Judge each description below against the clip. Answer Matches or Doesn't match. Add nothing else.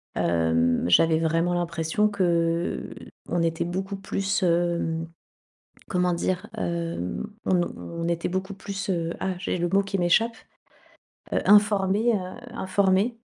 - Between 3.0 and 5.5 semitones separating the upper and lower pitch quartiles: Doesn't match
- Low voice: Doesn't match